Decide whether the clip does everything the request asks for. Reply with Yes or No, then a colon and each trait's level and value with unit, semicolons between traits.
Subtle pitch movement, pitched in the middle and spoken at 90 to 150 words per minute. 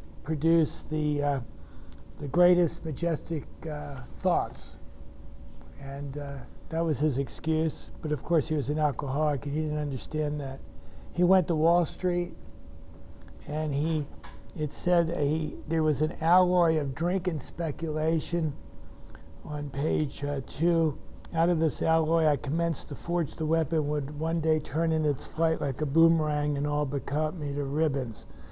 No: narrow, 2.3 semitones; medium, 155 Hz; average, 160 wpm